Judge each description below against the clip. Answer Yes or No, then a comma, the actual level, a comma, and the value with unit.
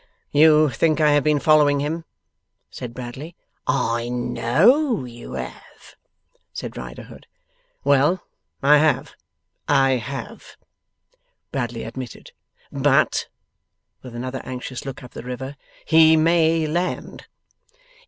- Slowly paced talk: Yes, slow, 110 wpm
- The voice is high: No, medium, 140 Hz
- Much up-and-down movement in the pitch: No, average, 4.0 semitones